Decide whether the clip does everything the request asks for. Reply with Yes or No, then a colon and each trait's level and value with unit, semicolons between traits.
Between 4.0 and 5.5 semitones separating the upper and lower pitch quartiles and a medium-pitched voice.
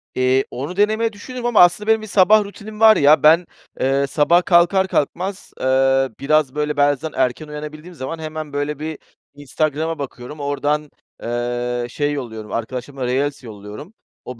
Yes: average, 4.7 semitones; medium, 150 Hz